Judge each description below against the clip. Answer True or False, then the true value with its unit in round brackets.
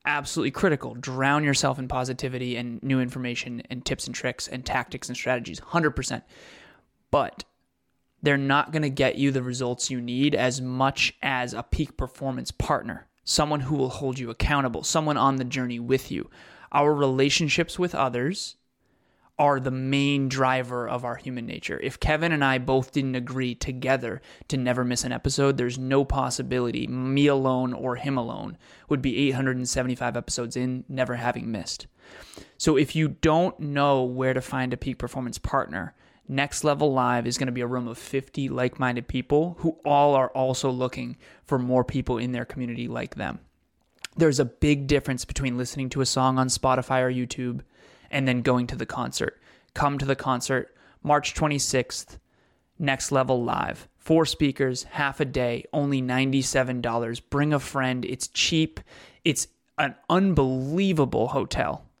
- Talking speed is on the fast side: False (165 wpm)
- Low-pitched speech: True (130 Hz)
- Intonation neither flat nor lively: False (2.1 semitones)